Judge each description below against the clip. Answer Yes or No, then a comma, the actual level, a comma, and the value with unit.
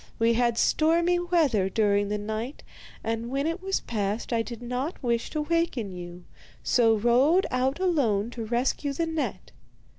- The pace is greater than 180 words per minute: No, average, 160 wpm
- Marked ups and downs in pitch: Yes, wide, 5.8 semitones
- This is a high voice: Yes, high, 240 Hz